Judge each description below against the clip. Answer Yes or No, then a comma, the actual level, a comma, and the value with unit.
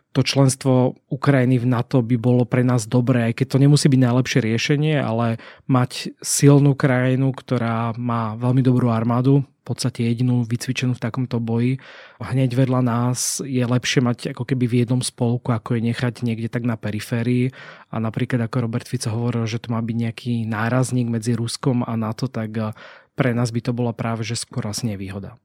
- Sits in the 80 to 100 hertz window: No, low, 125 Hz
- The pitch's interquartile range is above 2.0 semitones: No, narrow, 1.7 semitones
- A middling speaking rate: No, fast, 180 wpm